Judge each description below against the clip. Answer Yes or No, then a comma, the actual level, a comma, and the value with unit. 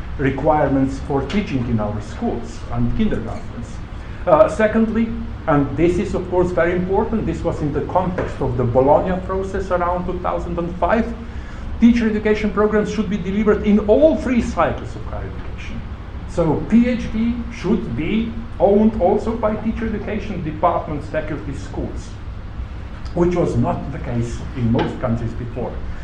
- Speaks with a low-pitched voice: No, medium, 170 Hz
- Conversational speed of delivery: Yes, average, 145 wpm